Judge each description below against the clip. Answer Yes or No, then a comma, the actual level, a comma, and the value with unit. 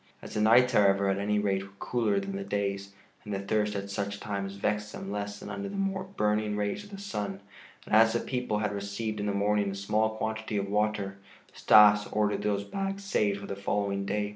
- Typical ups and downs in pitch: No, narrow, 1.5 semitones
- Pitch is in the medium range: No, low, 105 Hz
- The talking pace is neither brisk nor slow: No, fast, 215 wpm